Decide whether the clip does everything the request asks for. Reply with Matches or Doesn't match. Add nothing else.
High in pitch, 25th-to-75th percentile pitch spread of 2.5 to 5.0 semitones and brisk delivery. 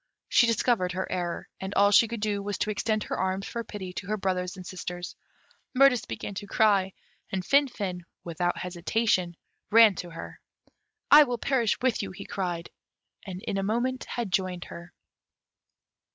Doesn't match